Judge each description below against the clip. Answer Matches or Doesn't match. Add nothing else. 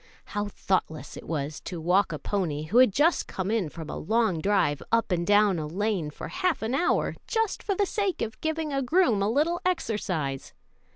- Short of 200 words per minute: Doesn't match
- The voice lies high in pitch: Matches